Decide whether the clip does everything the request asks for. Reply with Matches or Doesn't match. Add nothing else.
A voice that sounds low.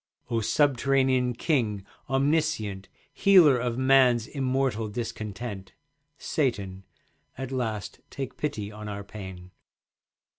Matches